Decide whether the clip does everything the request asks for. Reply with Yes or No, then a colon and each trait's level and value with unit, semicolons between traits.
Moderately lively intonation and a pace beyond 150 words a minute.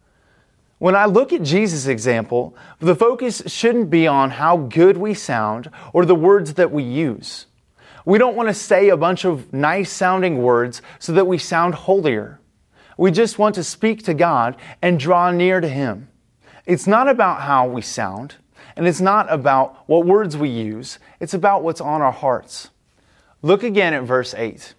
No: wide, 6.1 semitones; average, 180 wpm